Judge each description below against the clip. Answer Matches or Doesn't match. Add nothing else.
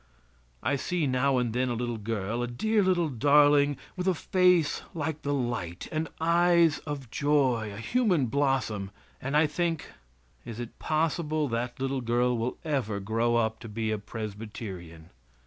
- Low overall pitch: Matches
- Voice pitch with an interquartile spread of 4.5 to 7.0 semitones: Matches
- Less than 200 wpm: Matches